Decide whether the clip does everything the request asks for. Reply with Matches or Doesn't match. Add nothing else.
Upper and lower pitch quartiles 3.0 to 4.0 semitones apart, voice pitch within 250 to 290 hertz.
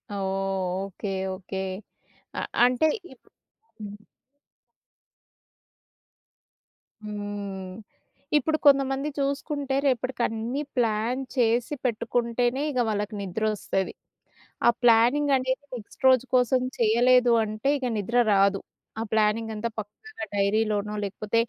Doesn't match